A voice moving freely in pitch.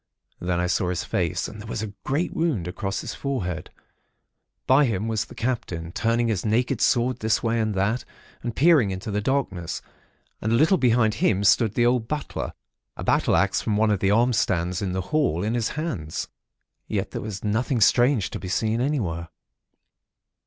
No: average, 4.4 semitones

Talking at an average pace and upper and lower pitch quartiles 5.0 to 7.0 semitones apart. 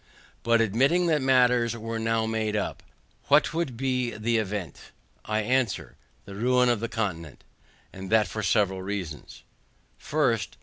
No: average, 145 wpm; average, 3.3 semitones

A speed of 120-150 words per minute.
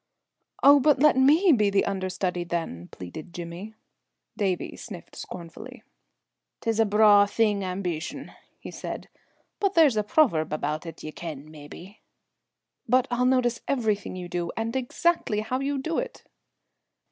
Yes: average, 145 wpm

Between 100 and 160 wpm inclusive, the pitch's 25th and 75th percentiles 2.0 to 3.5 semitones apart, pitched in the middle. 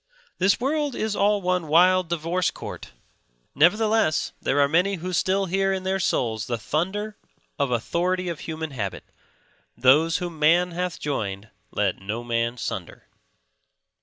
No: average, 145 wpm; average, 5.2 semitones; medium, 170 Hz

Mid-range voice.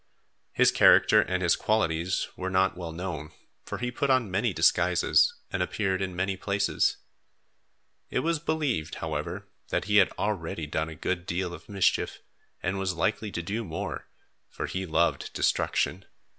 No: very low, 95 Hz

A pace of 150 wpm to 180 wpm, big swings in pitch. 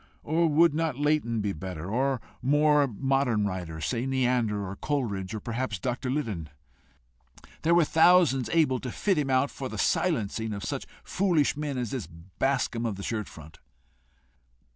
Yes: average, 165 wpm; wide, 6.1 semitones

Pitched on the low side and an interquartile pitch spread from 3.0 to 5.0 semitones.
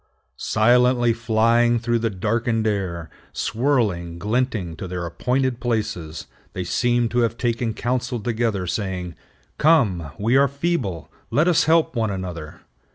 Yes: low, 115 Hz; average, 4.5 semitones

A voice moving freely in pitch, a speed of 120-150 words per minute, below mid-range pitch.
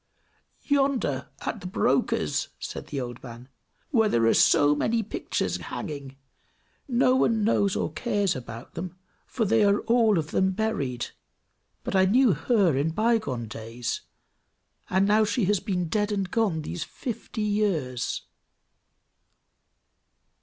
No: wide, 8.1 semitones; average, 140 wpm; high, 195 Hz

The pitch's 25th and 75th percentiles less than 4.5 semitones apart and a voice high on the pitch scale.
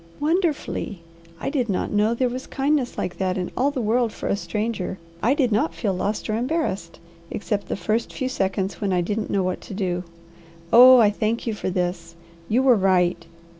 No: average, 5.0 semitones; high, 210 Hz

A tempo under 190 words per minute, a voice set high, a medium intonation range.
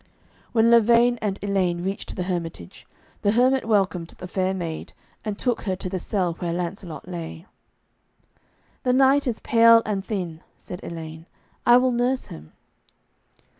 Yes: average, 150 wpm; high, 195 Hz; average, 5.0 semitones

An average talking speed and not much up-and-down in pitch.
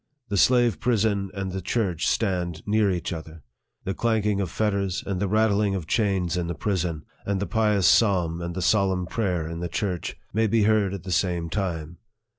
No: average, 190 wpm; average, 3.2 semitones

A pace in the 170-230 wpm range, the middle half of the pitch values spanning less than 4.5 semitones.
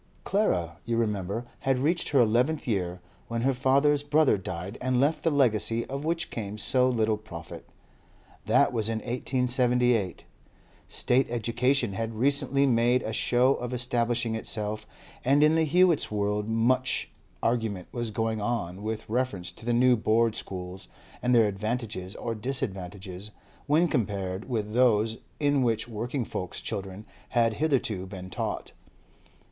No: average, 145 wpm; average, 3.5 semitones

